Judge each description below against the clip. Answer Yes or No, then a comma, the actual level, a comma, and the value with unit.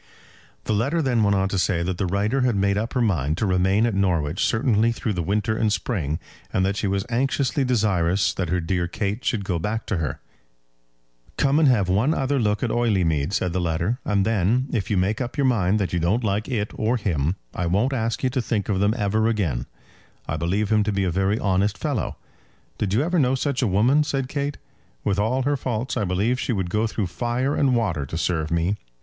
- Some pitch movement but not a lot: Yes, average, 4.5 semitones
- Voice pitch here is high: No, low, 105 Hz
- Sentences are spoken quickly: Yes, fast, 225 wpm